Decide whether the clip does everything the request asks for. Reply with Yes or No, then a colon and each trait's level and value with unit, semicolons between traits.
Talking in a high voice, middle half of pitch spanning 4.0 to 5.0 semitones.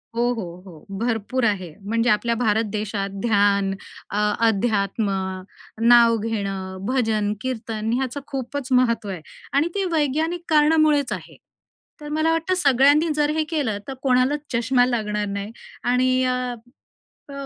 Yes: high, 240 Hz; average, 4.7 semitones